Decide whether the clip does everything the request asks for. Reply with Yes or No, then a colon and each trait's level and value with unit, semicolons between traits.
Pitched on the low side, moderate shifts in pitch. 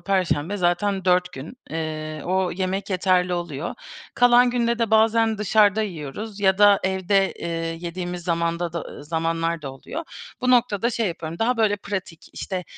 No: medium, 185 Hz; average, 3.9 semitones